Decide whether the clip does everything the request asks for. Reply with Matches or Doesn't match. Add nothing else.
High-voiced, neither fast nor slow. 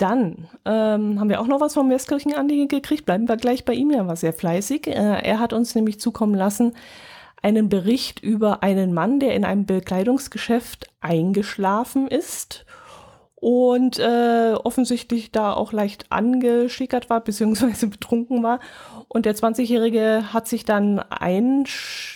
Matches